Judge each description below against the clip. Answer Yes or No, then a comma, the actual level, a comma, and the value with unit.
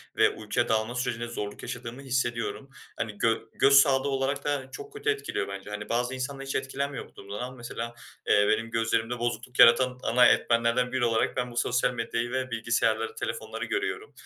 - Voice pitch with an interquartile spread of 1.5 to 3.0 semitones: Yes, narrow, 2.4 semitones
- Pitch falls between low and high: No, low, 120 Hz